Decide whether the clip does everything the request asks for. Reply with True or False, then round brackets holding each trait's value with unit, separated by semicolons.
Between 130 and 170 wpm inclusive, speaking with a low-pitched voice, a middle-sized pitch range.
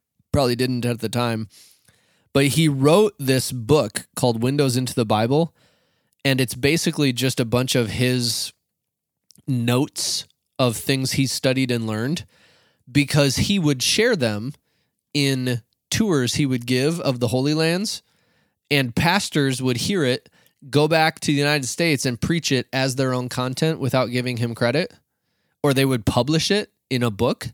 True (160 wpm; 130 Hz; 3.0 semitones)